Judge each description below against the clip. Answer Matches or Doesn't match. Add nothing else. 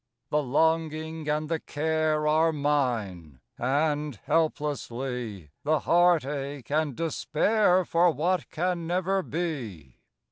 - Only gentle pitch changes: Doesn't match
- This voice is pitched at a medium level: Matches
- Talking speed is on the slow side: Matches